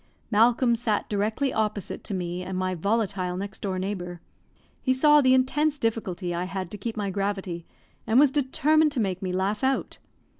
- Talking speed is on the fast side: No, average, 180 wpm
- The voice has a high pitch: Yes, high, 205 Hz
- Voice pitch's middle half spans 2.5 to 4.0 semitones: No, wide, 5.5 semitones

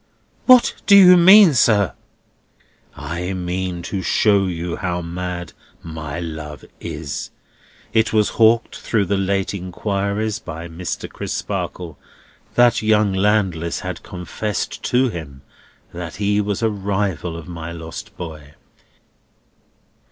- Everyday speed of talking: No, slow, 120 wpm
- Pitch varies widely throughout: No, average, 3.9 semitones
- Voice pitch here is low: Yes, very low, 95 Hz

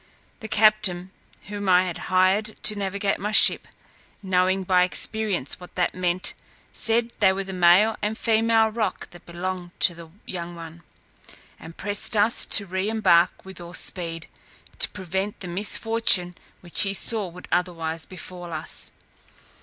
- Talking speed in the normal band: Yes, average, 155 wpm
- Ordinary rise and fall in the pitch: Yes, average, 3.0 semitones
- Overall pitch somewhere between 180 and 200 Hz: Yes, medium, 185 Hz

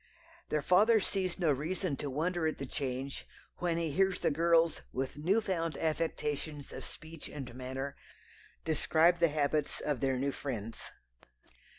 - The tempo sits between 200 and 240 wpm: No, average, 155 wpm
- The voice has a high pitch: No, medium, 155 Hz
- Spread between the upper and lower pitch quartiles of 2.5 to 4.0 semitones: Yes, average, 3.5 semitones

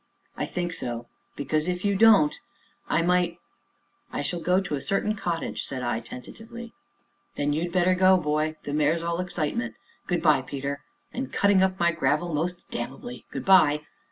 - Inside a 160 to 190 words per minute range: Yes, average, 180 wpm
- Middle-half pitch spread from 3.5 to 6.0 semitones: Yes, average, 4.1 semitones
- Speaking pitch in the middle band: Yes, medium, 170 Hz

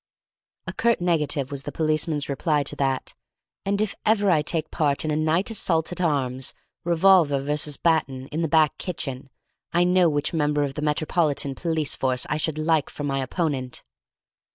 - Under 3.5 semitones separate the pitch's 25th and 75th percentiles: Yes, average, 3.0 semitones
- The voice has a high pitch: No, medium, 155 Hz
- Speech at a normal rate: Yes, average, 175 wpm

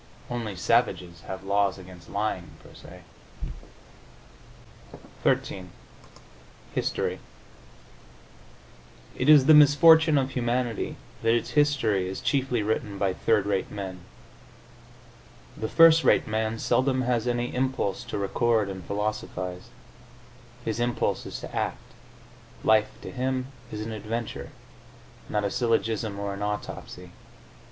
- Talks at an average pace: No, slow, 120 wpm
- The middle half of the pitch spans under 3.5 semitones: No, average, 4.1 semitones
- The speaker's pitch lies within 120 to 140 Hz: No, low, 110 Hz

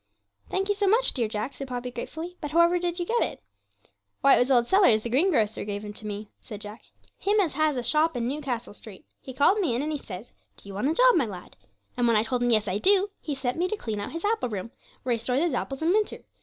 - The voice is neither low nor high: No, very high, 265 Hz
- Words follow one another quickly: Yes, fast, 270 wpm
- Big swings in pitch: Yes, wide, 7.5 semitones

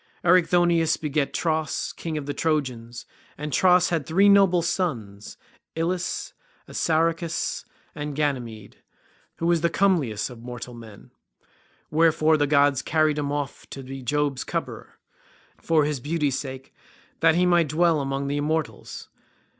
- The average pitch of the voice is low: No, medium, 150 Hz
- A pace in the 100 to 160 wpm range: Yes, average, 140 wpm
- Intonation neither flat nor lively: Yes, average, 3.5 semitones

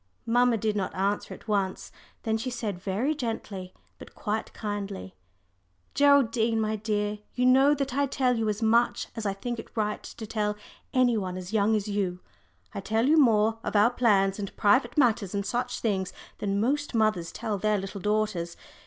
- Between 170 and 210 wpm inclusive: Yes, average, 185 wpm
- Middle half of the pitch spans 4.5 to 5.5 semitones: No, average, 3.1 semitones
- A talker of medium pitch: No, high, 215 Hz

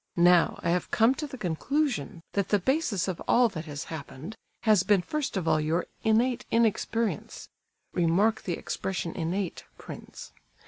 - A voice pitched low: No, high, 190 Hz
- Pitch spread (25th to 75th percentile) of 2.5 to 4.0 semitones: No, average, 5.3 semitones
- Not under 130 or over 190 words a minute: Yes, average, 155 wpm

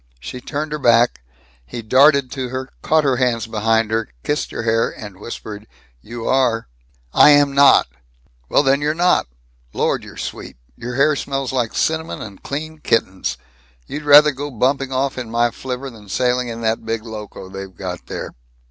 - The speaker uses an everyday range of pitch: Yes, average, 3.8 semitones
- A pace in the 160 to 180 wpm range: Yes, average, 175 wpm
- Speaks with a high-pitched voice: No, low, 125 Hz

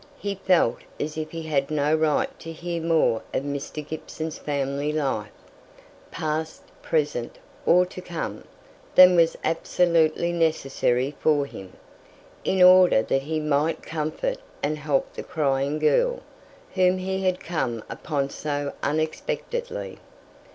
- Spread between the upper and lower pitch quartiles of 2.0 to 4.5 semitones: Yes, average, 3.5 semitones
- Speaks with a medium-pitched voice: Yes, medium, 155 Hz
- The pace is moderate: No, slow, 130 wpm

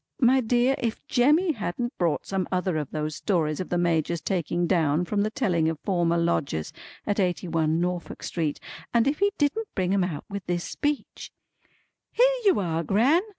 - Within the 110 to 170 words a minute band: No, average, 185 wpm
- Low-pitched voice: No, medium, 180 Hz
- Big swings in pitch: Yes, wide, 6.4 semitones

